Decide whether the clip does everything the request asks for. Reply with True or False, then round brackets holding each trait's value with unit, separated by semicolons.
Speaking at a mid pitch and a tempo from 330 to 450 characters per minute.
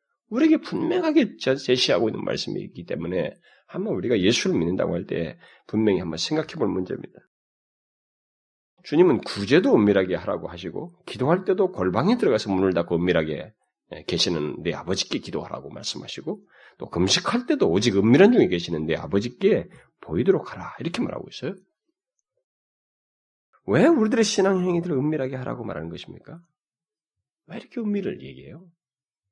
True (155 Hz; 360 characters per minute)